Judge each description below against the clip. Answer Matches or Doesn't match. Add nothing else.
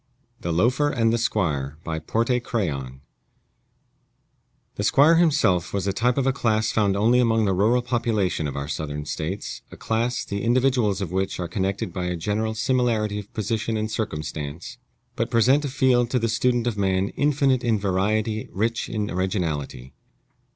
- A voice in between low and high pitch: Doesn't match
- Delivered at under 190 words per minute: Matches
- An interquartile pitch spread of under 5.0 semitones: Matches